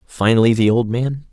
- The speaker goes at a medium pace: Yes, average, 180 wpm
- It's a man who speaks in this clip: Yes, male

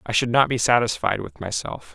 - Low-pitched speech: Yes, low, 120 Hz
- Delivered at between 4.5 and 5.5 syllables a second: Yes, 5.4 syllables/s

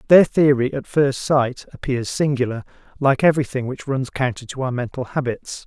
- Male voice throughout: Yes, male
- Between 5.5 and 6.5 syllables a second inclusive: No, 5.2 syllables/s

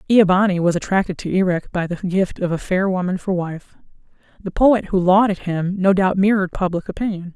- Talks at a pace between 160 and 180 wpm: No, fast, 205 wpm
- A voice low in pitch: No, medium, 185 Hz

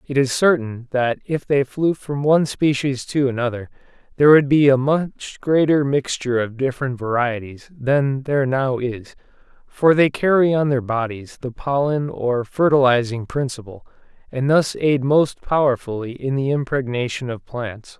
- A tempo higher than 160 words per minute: No, average, 155 wpm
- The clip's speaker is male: Yes, male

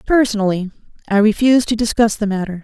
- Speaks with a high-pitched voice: Yes, high, 215 Hz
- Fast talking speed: No, average, 160 wpm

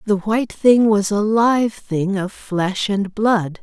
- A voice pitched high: Yes, high, 205 Hz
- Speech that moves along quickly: No, average, 180 wpm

